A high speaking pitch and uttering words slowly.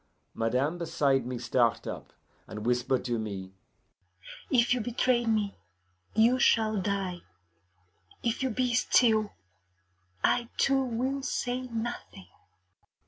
Yes: high, 215 Hz; slow, 115 wpm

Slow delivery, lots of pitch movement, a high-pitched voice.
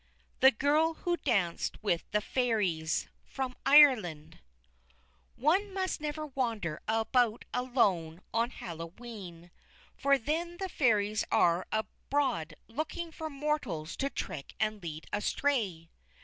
Yes: slow, 115 wpm; wide, 8.5 semitones; high, 230 Hz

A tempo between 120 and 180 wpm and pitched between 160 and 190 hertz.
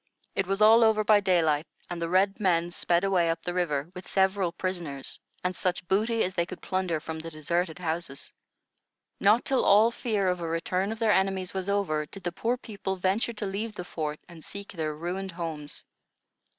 No: average, 200 wpm; medium, 185 Hz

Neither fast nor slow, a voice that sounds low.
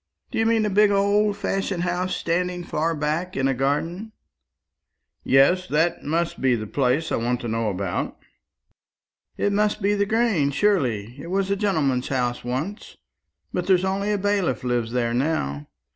No: average, 170 wpm; medium, 170 Hz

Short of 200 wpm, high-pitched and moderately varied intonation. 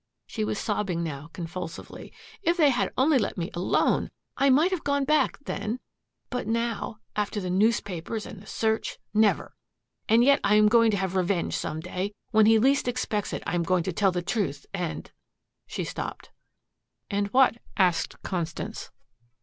Yes: average, 175 wpm; high, 210 Hz; average, 4.6 semitones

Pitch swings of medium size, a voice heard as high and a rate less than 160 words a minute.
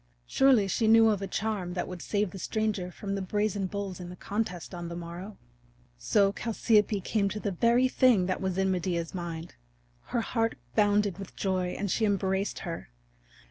No: average, 3.0 semitones; high, 195 Hz; average, 185 wpm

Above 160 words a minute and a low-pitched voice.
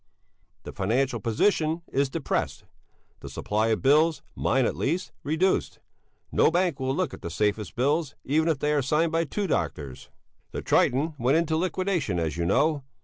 No: average, 170 wpm; medium, 145 Hz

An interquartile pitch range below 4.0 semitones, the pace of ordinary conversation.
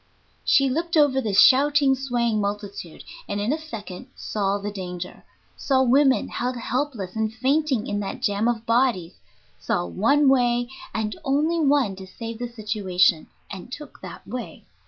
No: average, 4.8 semitones; average, 155 wpm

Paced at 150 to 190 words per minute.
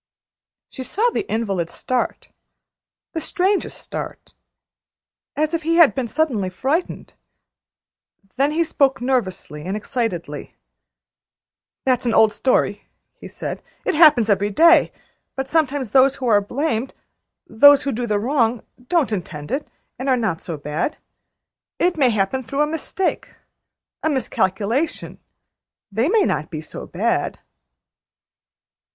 No: slow, 135 wpm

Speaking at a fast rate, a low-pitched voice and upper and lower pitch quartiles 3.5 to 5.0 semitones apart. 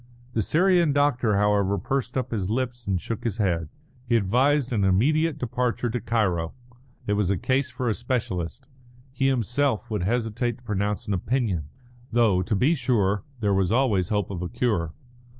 No: average, 175 wpm; low, 115 Hz; average, 4.4 semitones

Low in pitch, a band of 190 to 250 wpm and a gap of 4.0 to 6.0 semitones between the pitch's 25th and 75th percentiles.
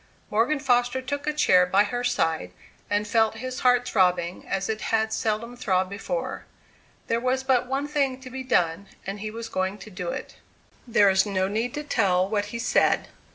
No: high, 220 Hz; average, 195 wpm; average, 4.6 semitones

